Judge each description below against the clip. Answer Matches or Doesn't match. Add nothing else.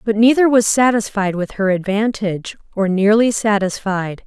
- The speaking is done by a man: Doesn't match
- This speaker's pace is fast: Doesn't match